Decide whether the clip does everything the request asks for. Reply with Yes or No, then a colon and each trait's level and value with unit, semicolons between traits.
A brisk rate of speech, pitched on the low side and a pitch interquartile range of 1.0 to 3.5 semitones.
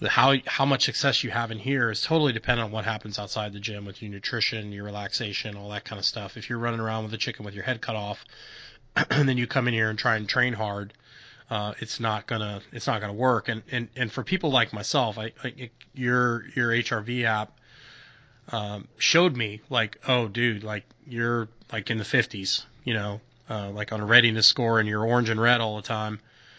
Yes: fast, 225 wpm; low, 115 Hz; average, 2.7 semitones